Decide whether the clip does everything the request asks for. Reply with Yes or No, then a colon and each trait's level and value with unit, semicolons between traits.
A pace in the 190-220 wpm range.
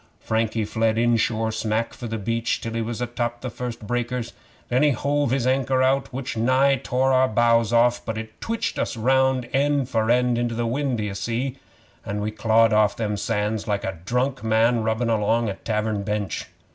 Yes: average, 195 wpm